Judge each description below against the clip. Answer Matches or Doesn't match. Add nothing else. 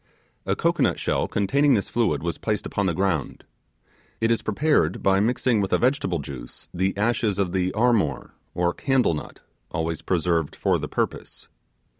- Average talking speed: Matches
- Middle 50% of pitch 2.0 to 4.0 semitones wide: Doesn't match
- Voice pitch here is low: Matches